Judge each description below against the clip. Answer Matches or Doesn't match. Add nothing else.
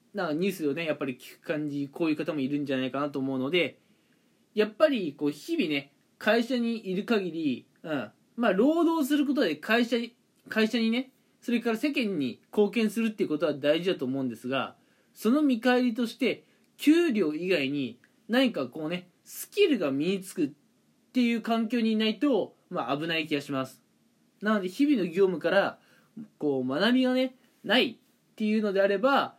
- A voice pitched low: Doesn't match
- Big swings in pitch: Matches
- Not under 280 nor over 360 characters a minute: Matches